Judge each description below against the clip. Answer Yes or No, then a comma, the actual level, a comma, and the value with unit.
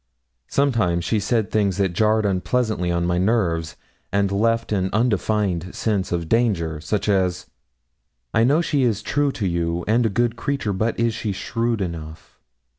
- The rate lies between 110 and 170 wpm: Yes, average, 160 wpm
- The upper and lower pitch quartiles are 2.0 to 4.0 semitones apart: No, average, 4.4 semitones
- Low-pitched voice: Yes, low, 105 Hz